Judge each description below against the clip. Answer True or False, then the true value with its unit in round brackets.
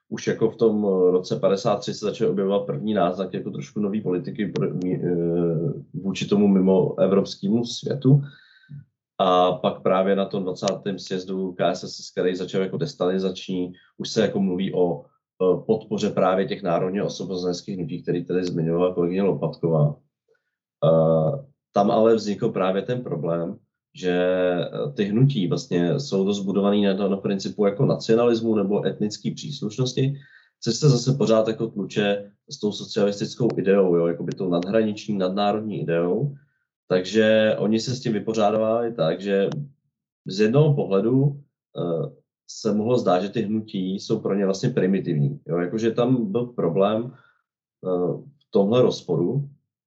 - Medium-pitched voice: False (100 Hz)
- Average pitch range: True (4.5 semitones)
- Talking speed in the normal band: True (140 wpm)